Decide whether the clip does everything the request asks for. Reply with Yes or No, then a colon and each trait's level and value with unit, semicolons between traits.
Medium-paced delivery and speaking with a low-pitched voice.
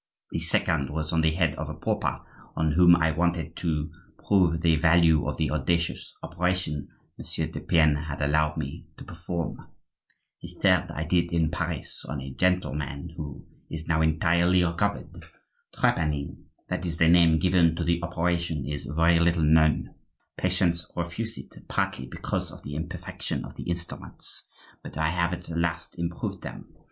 Yes: average, 160 wpm; very low, 85 Hz